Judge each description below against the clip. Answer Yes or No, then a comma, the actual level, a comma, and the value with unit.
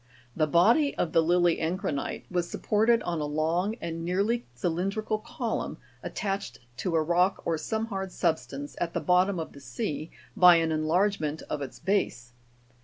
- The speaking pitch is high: No, medium, 175 Hz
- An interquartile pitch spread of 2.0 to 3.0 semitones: No, average, 3.9 semitones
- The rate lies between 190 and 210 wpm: No, average, 165 wpm